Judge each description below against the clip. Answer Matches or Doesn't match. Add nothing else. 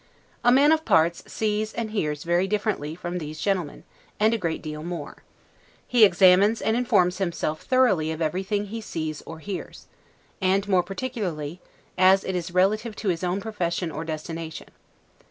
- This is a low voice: Doesn't match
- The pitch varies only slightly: Doesn't match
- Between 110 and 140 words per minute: Doesn't match